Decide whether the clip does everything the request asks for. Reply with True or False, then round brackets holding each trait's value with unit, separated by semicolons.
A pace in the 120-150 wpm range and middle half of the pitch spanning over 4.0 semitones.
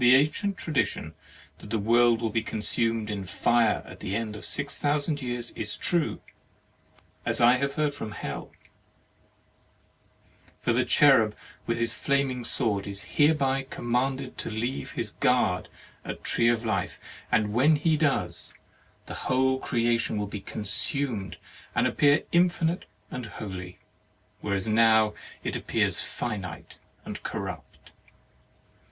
True (140 wpm; 4.5 semitones)